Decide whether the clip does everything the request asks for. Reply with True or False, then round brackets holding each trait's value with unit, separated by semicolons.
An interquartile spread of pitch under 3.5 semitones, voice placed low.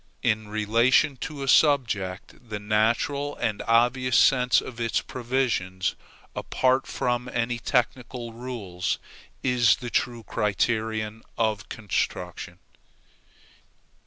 True (2.9 semitones; 115 Hz)